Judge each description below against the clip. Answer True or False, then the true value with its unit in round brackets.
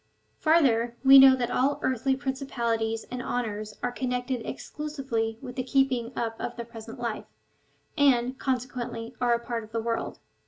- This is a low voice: False (245 Hz)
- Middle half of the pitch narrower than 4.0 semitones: True (2.5 semitones)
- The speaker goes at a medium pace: True (165 wpm)